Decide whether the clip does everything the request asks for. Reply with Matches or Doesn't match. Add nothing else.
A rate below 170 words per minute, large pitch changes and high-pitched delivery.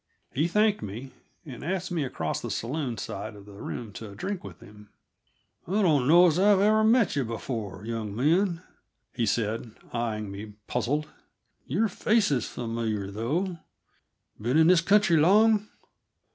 Doesn't match